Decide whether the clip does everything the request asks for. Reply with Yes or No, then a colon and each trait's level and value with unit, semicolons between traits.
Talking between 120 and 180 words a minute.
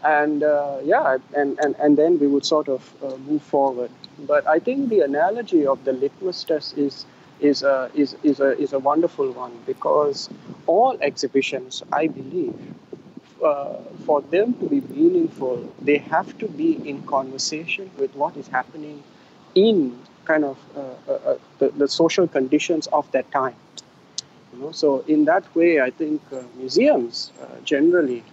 Yes: average, 165 wpm